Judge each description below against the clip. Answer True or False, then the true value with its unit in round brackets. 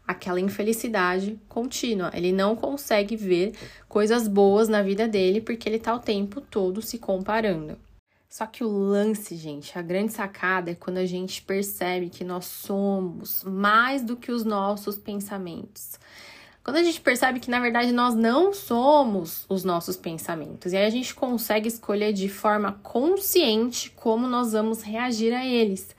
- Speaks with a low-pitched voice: False (210 Hz)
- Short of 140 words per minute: False (160 wpm)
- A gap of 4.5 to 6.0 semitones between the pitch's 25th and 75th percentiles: False (3.6 semitones)